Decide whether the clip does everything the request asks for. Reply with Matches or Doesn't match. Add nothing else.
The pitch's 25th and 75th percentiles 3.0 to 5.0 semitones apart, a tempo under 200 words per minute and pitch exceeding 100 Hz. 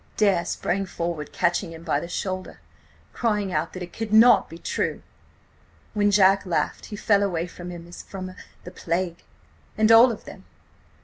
Matches